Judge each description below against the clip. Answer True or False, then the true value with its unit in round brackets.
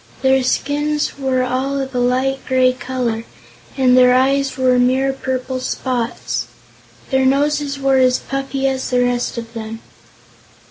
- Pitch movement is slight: True (1.4 semitones)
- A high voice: True (260 Hz)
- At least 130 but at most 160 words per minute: True (145 wpm)